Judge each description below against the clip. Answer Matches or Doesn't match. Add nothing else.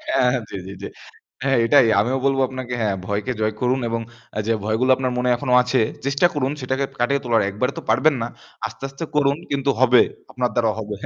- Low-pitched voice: Matches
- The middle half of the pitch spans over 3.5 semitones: Doesn't match